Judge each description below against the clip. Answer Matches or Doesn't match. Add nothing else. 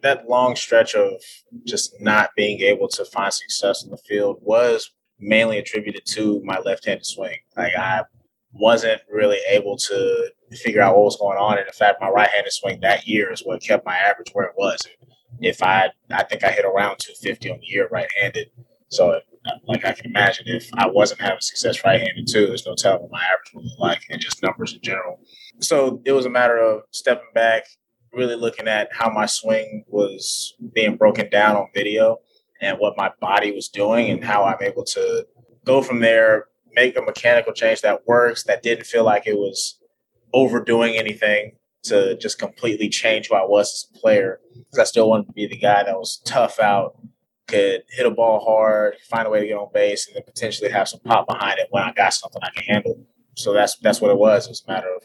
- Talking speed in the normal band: Doesn't match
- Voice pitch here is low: Matches